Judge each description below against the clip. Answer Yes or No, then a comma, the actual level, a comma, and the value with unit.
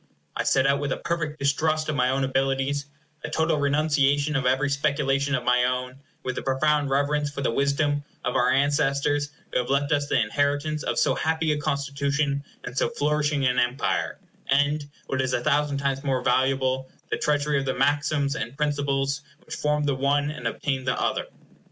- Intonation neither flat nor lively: No, narrow, 1.6 semitones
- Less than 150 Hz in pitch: Yes, medium, 140 Hz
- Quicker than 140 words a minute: Yes, average, 195 wpm